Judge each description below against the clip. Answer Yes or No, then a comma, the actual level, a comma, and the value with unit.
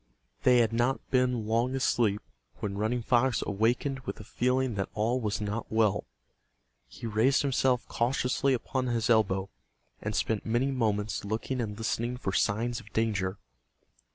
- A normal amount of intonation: Yes, average, 3.0 semitones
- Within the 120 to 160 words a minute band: Yes, average, 155 wpm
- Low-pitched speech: Yes, low, 115 Hz